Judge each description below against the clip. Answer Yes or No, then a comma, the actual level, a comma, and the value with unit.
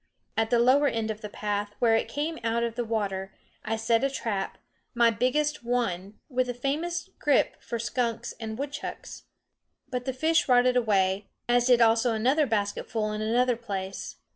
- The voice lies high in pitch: Yes, high, 235 Hz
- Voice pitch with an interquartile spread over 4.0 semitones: No, average, 2.7 semitones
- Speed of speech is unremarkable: Yes, average, 175 wpm